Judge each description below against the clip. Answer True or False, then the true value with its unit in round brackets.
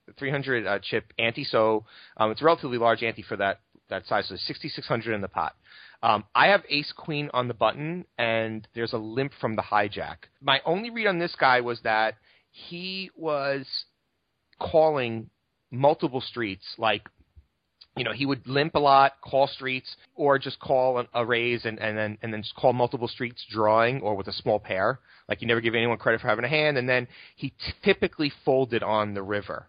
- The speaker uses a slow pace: False (190 wpm)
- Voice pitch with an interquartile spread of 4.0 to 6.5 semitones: True (4.3 semitones)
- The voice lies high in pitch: False (120 Hz)